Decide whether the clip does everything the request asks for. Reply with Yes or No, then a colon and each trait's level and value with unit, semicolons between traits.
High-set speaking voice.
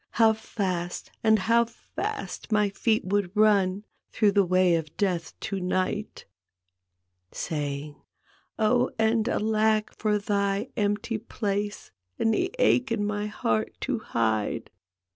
Yes: high, 205 Hz